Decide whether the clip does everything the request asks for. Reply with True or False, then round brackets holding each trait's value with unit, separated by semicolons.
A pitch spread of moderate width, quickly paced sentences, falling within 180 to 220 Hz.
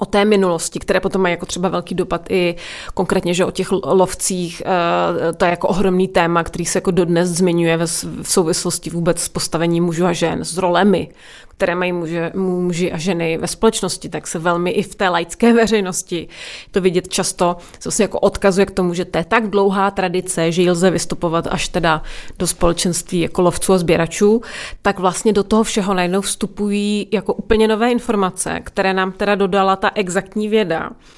False (2.3 semitones; 185 wpm; 185 Hz)